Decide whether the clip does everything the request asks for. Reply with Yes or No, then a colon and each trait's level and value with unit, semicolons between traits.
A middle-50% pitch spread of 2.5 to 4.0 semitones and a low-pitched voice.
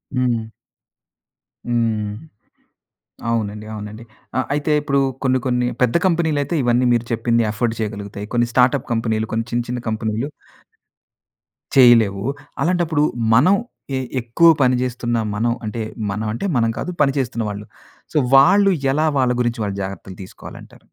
Yes: average, 3.1 semitones; low, 120 Hz